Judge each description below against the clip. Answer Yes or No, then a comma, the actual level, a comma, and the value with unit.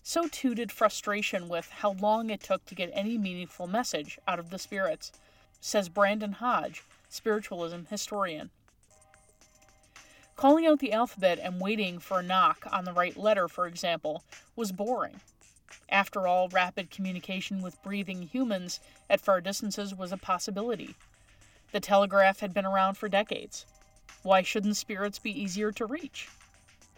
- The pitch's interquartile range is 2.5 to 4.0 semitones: Yes, average, 2.8 semitones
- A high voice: Yes, high, 195 Hz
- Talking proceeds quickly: No, average, 150 wpm